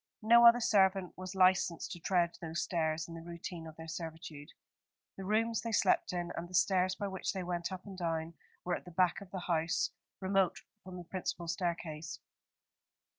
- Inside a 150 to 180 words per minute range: No, average, 190 wpm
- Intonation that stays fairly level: Yes, narrow, 2.3 semitones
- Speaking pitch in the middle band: Yes, medium, 180 Hz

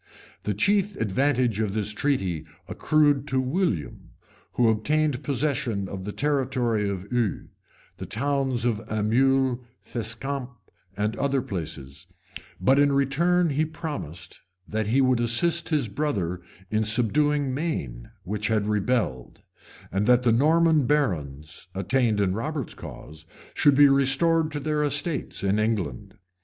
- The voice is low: Yes, low, 125 Hz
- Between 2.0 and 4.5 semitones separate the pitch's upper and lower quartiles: No, wide, 5.6 semitones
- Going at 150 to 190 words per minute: No, slow, 135 wpm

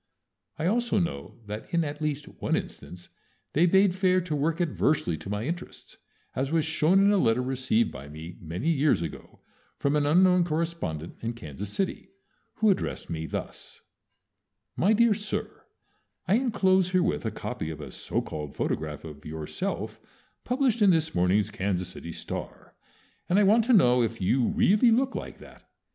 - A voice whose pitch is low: No, medium, 155 Hz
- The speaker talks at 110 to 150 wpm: No, average, 170 wpm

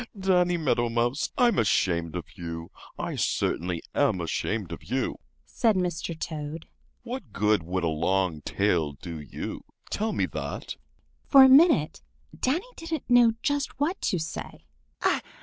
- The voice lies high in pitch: No, low, 135 Hz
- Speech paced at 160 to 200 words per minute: No, average, 145 wpm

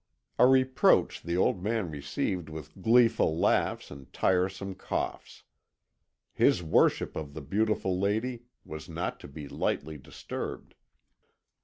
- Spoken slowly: Yes, slow, 125 wpm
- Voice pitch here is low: Yes, very low, 90 Hz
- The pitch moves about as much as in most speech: No, wide, 6.0 semitones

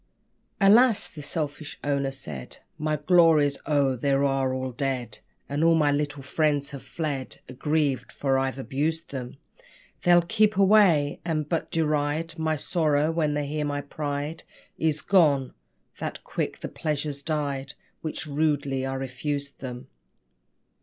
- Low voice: No, medium, 145 Hz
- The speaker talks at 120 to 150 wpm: Yes, average, 140 wpm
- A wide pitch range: No, narrow, 2.5 semitones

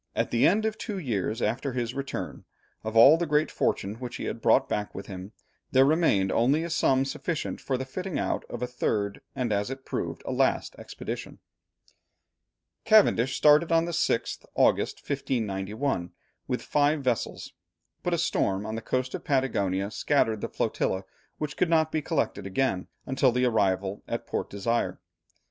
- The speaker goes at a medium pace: Yes, average, 175 wpm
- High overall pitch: No, low, 130 Hz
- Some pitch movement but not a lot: No, wide, 6.0 semitones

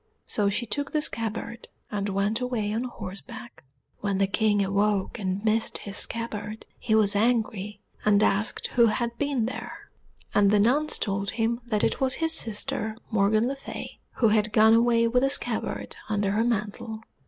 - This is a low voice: No, high, 220 Hz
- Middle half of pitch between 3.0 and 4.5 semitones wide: No, narrow, 2.4 semitones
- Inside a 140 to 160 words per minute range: No, average, 175 wpm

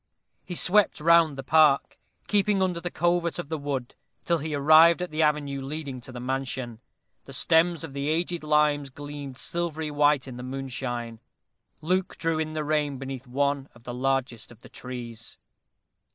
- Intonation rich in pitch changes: No, average, 3.5 semitones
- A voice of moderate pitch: Yes, medium, 145 Hz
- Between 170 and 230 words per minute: Yes, average, 175 wpm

